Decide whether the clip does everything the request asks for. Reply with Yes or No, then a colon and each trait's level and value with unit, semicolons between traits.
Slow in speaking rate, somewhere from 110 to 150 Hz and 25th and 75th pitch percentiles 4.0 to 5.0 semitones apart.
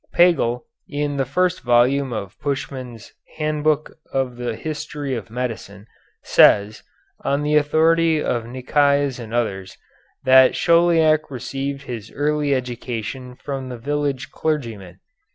No: slow, 120 wpm; low, 135 Hz; average, 3.6 semitones